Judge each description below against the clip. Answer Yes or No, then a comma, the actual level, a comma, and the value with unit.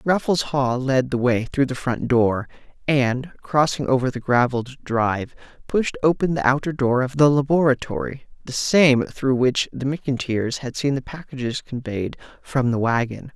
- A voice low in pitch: Yes, low, 130 Hz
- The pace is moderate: Yes, average, 160 wpm